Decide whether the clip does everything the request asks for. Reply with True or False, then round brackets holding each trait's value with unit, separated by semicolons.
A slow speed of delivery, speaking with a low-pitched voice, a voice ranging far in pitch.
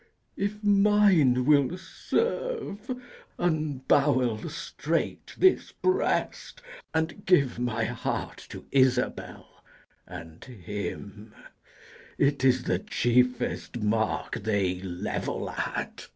True (90 wpm; 130 Hz; 8.9 semitones)